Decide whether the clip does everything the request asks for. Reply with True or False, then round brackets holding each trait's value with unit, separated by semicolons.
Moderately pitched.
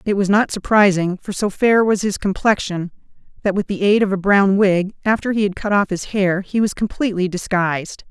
False (195 Hz)